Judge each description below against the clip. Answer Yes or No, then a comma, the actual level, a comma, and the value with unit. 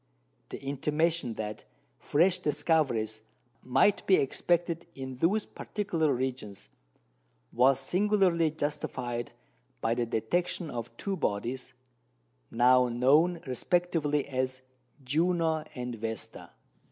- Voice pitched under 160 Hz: Yes, medium, 140 Hz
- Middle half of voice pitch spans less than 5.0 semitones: No, wide, 5.4 semitones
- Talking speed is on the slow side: Yes, slow, 100 wpm